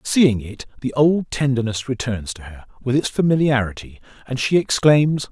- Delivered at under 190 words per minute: Yes, average, 160 wpm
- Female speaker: No, male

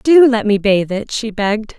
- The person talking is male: No, female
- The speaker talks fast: Yes, fast, 235 wpm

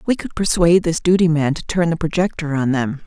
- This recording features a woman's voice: Yes, female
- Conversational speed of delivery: No, fast, 255 wpm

